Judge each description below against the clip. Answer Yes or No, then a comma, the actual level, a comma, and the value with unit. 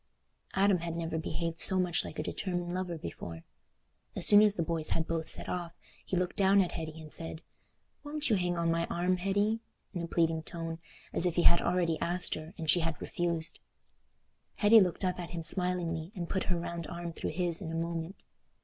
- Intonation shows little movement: Yes, narrow, 1.7 semitones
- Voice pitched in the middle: Yes, medium, 170 Hz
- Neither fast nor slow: No, fast, 210 wpm